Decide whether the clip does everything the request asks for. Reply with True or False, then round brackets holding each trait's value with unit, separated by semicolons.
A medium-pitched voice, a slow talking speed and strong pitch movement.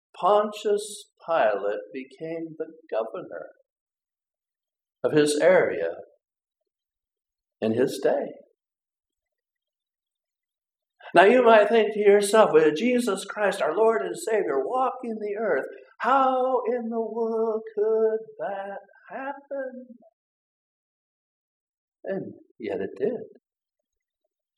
False (230 Hz; 95 wpm; 7.2 semitones)